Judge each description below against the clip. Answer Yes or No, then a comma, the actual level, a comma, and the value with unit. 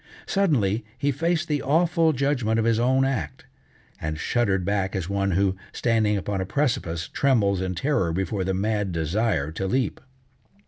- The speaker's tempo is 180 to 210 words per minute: No, average, 165 wpm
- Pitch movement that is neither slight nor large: No, wide, 5.9 semitones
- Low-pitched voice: Yes, low, 105 Hz